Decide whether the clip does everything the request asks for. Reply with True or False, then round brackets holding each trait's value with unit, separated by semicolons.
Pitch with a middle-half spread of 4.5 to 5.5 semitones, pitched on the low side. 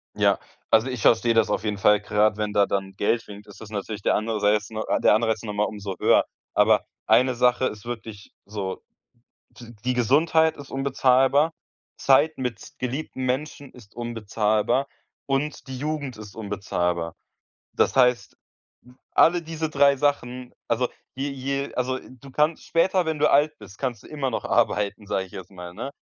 True (4.8 semitones; 120 Hz)